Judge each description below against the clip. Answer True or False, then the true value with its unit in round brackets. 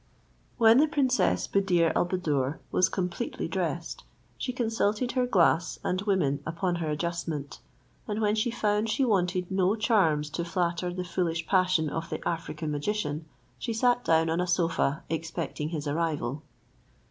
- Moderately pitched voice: True (175 Hz)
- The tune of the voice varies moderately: True (4.4 semitones)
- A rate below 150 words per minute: False (155 wpm)